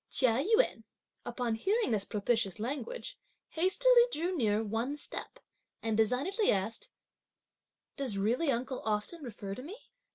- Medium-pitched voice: No, very high, 250 Hz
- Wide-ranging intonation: Yes, wide, 7.5 semitones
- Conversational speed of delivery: No, slow, 130 wpm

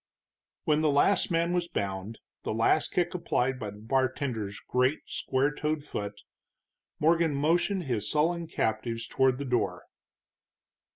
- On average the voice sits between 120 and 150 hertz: Yes, low, 135 Hz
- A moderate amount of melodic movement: No, wide, 5.8 semitones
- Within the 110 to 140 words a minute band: Yes, slow, 135 wpm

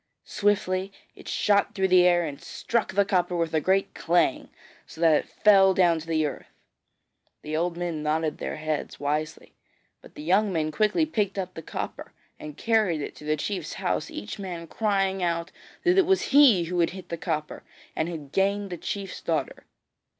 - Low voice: No, medium, 175 Hz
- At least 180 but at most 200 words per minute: Yes, average, 190 wpm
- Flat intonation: No, average, 3.9 semitones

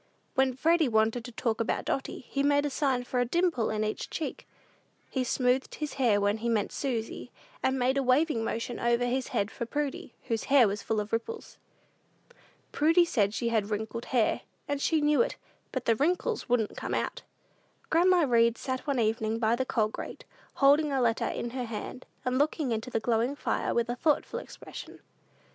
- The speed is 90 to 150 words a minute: No, average, 195 wpm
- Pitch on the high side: Yes, high, 245 Hz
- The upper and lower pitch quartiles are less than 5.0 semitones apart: Yes, average, 3.9 semitones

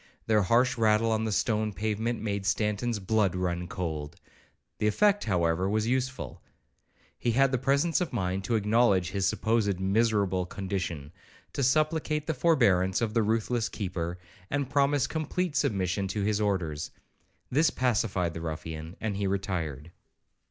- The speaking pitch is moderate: No, low, 105 Hz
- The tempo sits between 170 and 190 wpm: No, average, 150 wpm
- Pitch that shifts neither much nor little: Yes, average, 4.6 semitones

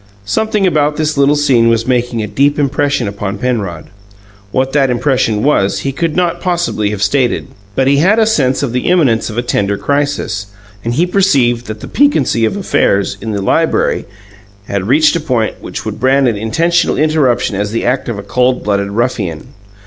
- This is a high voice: No, low, 125 Hz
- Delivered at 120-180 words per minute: No, average, 190 wpm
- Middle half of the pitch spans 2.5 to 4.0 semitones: No, wide, 5.4 semitones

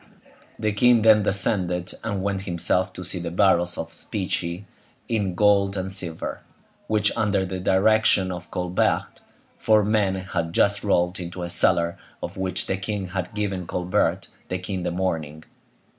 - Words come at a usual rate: Yes, average, 160 wpm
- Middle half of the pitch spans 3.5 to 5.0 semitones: No, narrow, 2.5 semitones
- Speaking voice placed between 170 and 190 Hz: No, very low, 95 Hz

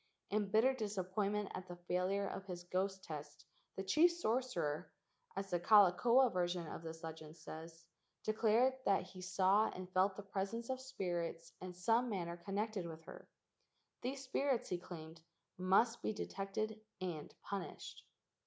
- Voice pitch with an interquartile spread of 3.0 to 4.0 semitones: Yes, average, 3.6 semitones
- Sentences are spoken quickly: No, average, 155 wpm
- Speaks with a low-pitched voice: No, high, 190 Hz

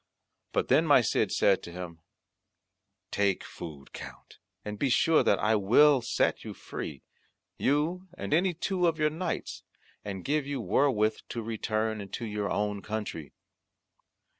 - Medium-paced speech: Yes, average, 150 wpm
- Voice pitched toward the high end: No, low, 110 Hz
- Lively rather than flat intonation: Yes, wide, 6.6 semitones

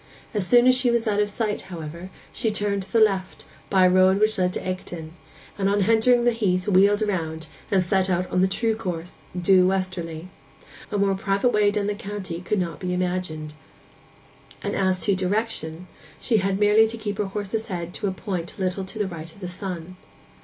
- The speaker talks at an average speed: No, fast, 210 wpm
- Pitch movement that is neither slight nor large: No, narrow, 2.3 semitones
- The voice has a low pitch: No, high, 190 Hz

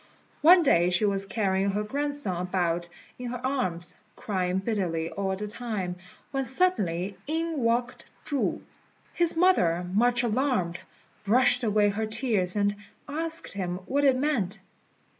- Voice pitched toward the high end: Yes, high, 210 Hz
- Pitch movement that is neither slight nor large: No, wide, 6.2 semitones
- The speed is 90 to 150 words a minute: Yes, average, 140 wpm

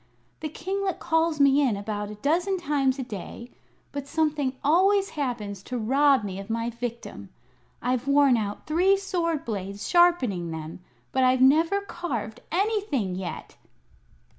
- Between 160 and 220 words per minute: No, average, 145 wpm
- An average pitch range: No, wide, 7.2 semitones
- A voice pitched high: Yes, very high, 270 Hz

